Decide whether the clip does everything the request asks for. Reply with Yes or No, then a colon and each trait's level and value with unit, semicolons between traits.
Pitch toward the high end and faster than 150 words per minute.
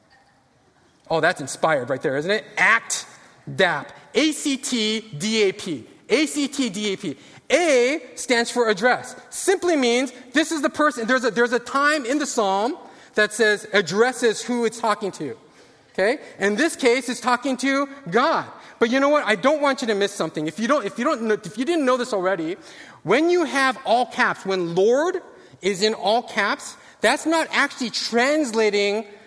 Yes: high, 245 Hz; average, 190 wpm